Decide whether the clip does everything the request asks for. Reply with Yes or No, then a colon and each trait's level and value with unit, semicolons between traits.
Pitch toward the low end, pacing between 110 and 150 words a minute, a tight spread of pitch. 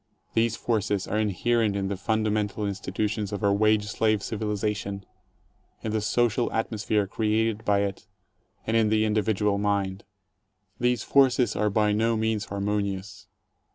Yes: low, 105 Hz; average, 140 wpm; narrow, 1.6 semitones